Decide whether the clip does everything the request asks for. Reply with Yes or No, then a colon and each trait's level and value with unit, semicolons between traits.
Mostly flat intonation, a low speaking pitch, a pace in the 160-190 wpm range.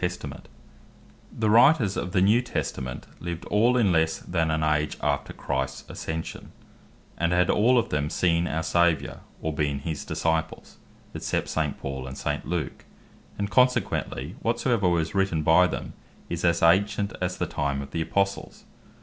No: average, 4.0 semitones; very low, 85 Hz; average, 165 wpm